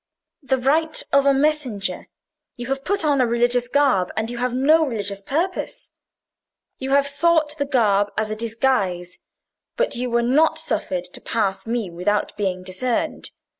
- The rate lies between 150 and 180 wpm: Yes, average, 165 wpm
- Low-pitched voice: No, high, 245 Hz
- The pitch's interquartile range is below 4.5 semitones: No, wide, 5.4 semitones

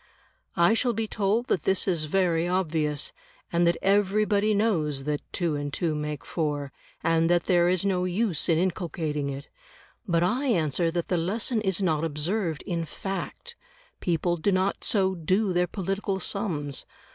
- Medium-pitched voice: Yes, medium, 175 Hz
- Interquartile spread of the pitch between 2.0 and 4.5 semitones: Yes, average, 3.7 semitones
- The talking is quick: No, average, 165 wpm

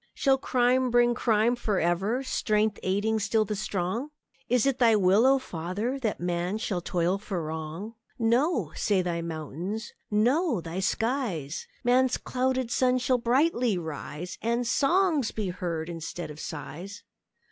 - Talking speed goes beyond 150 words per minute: No, average, 145 wpm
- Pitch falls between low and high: No, high, 215 Hz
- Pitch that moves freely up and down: Yes, wide, 5.9 semitones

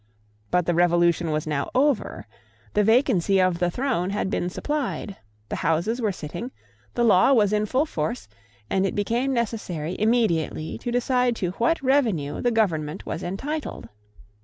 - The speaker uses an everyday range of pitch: No, wide, 5.9 semitones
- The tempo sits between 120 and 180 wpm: Yes, average, 160 wpm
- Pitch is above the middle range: Yes, high, 200 Hz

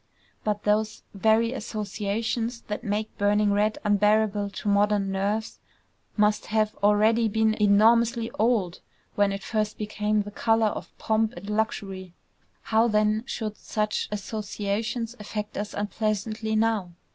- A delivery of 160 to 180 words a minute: No, slow, 135 wpm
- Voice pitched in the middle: No, high, 210 Hz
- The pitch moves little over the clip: Yes, narrow, 1.2 semitones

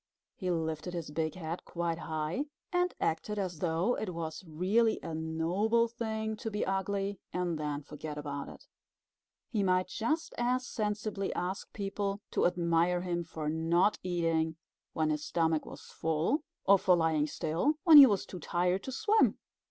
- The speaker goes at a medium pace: Yes, average, 165 wpm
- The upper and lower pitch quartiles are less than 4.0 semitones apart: No, average, 4.4 semitones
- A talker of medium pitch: Yes, medium, 180 Hz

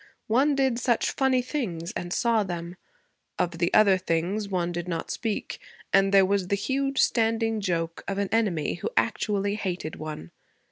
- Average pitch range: Yes, average, 4.6 semitones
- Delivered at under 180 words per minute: Yes, average, 170 wpm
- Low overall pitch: No, high, 195 Hz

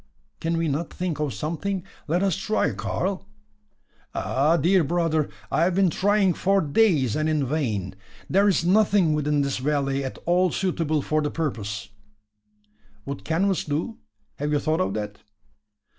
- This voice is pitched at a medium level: Yes, medium, 160 Hz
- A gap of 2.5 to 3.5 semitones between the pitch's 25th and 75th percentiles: No, average, 4.3 semitones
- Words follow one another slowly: No, average, 160 wpm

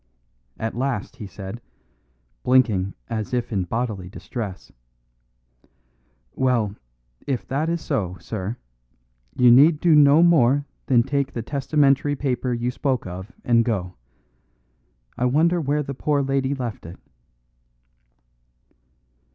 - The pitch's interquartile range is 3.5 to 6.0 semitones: Yes, average, 4.2 semitones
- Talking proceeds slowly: Yes, slow, 120 wpm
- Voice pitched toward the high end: No, low, 125 Hz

